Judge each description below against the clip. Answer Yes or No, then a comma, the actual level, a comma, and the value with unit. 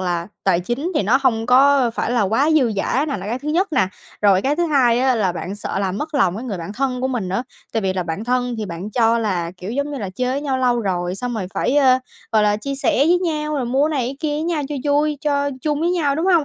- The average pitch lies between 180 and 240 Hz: No, very high, 250 Hz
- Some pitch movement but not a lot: No, wide, 5.9 semitones